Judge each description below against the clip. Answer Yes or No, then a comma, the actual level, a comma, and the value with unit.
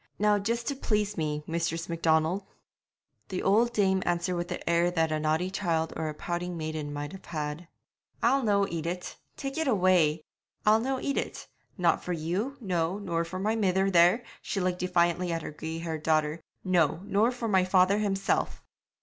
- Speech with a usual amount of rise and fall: Yes, average, 3.6 semitones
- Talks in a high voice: No, medium, 180 Hz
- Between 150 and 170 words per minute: No, average, 185 wpm